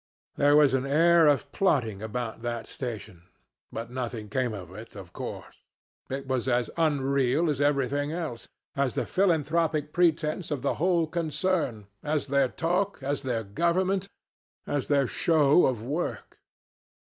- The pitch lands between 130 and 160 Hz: Yes, medium, 140 Hz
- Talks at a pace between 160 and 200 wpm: No, average, 145 wpm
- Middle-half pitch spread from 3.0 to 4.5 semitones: No, average, 4.9 semitones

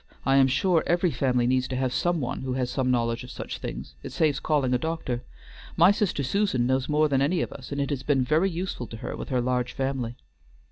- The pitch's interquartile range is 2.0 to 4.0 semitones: Yes, average, 3.6 semitones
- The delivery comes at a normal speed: No, fast, 240 wpm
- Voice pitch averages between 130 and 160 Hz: Yes, low, 135 Hz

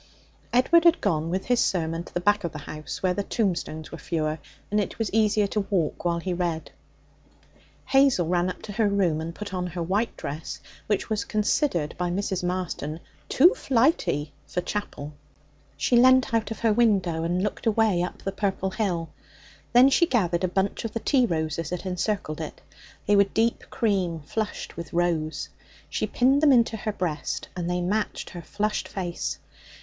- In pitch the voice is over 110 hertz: Yes, high, 190 Hz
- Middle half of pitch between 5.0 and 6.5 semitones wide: No, average, 4.3 semitones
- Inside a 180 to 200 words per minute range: Yes, average, 185 wpm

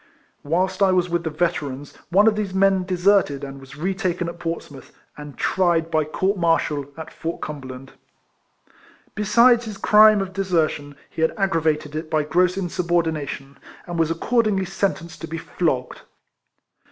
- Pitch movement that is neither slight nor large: Yes, average, 3.9 semitones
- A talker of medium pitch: Yes, medium, 170 Hz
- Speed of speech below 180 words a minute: Yes, average, 165 wpm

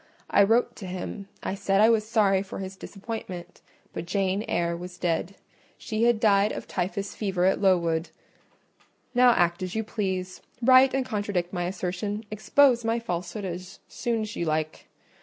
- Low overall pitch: No, high, 195 Hz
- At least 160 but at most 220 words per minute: Yes, average, 165 wpm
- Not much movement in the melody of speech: No, average, 3.4 semitones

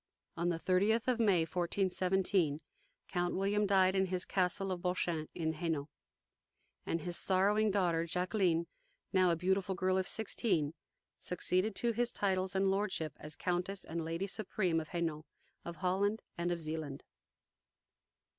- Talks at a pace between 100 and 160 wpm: Yes, average, 145 wpm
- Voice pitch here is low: No, medium, 185 Hz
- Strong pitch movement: No, narrow, 2.6 semitones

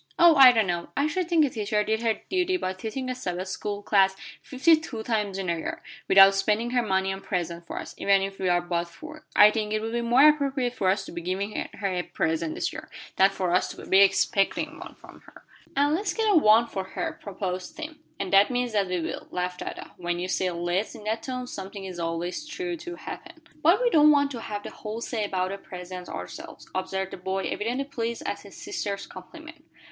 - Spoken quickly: Yes, fast, 235 wpm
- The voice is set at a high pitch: Yes, high, 205 Hz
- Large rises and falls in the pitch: Yes, wide, 5.7 semitones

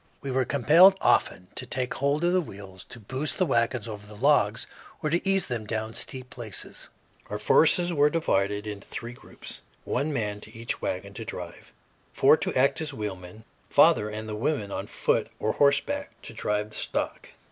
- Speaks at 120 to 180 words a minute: No, average, 190 wpm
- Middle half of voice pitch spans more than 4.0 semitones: Yes, wide, 5.6 semitones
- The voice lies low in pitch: Yes, low, 115 Hz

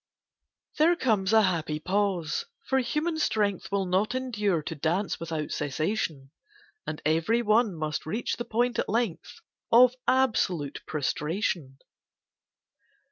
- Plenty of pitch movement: Yes, wide, 6.6 semitones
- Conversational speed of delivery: No, slow, 125 wpm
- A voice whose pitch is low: No, high, 195 Hz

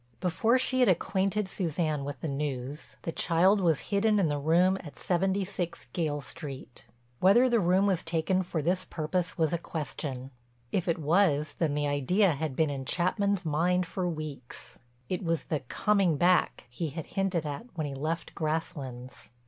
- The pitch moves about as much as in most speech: Yes, average, 4.2 semitones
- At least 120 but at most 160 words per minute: No, average, 170 wpm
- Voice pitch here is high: No, medium, 165 Hz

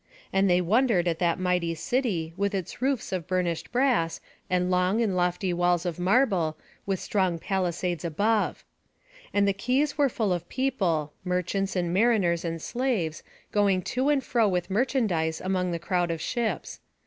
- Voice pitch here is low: No, medium, 185 Hz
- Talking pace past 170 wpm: No, average, 165 wpm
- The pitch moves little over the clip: No, average, 4.2 semitones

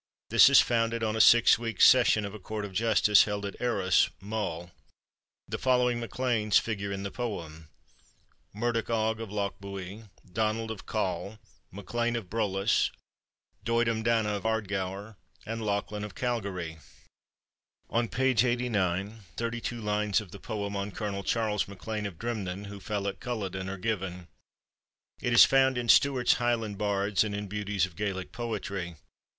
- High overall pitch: No, low, 105 Hz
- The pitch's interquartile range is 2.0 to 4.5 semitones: Yes, average, 2.7 semitones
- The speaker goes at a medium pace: Yes, average, 155 wpm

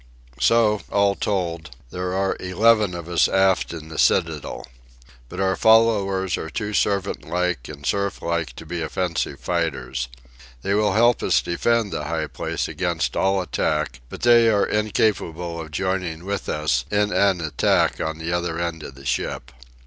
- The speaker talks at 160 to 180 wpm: Yes, average, 165 wpm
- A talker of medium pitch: No, very low, 90 Hz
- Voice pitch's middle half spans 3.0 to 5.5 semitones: Yes, average, 3.7 semitones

